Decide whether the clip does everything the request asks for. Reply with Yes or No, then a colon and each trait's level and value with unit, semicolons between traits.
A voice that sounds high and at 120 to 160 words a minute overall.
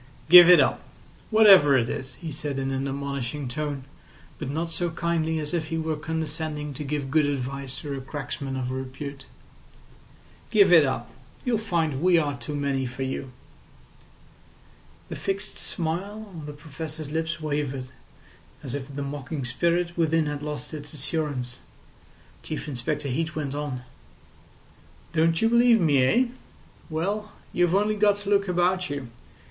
No: medium, 150 Hz; average, 155 wpm